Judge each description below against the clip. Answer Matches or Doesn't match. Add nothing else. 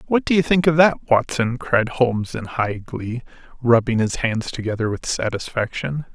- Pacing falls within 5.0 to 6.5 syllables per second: Doesn't match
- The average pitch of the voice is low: Matches